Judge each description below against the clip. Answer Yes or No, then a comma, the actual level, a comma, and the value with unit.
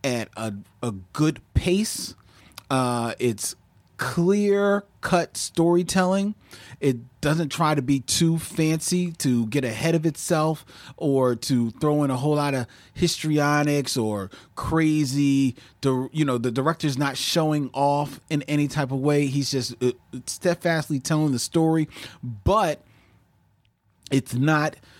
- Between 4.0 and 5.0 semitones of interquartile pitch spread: Yes, average, 4.3 semitones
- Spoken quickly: No, slow, 135 wpm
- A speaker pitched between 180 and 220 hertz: No, medium, 140 Hz